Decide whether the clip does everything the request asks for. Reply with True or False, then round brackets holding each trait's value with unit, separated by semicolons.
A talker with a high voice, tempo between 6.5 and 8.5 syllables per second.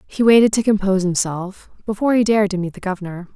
True (200 Hz; 6.9 syllables/s)